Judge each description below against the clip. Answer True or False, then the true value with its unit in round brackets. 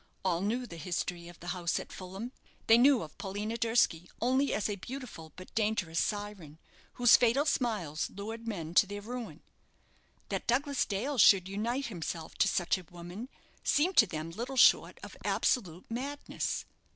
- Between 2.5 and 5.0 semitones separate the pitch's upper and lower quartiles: False (5.5 semitones)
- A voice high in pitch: True (210 Hz)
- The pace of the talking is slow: False (165 wpm)